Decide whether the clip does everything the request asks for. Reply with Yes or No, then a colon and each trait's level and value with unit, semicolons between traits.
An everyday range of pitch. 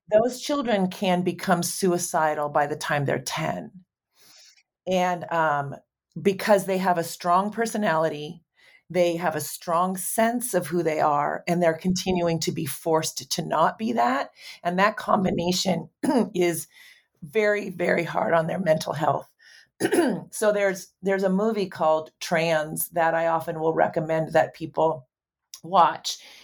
Yes: average, 3.2 semitones